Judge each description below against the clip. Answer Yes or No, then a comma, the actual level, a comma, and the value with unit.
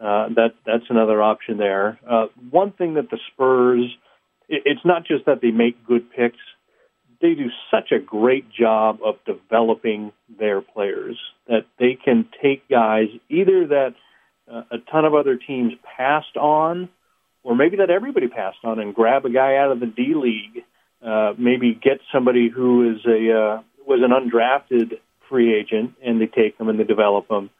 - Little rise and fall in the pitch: No, average, 3.8 semitones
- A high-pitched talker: No, low, 120 Hz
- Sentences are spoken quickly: No, average, 180 wpm